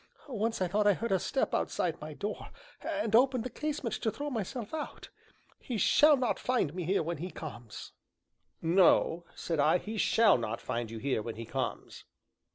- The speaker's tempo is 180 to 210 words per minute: Yes, average, 185 wpm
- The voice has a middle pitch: No, high, 200 Hz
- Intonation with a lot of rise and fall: Yes, wide, 7.8 semitones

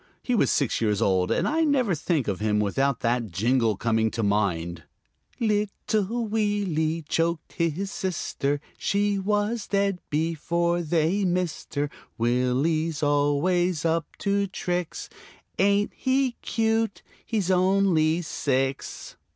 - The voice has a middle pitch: Yes, medium, 165 Hz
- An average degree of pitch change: No, wide, 6.8 semitones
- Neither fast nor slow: No, slow, 125 wpm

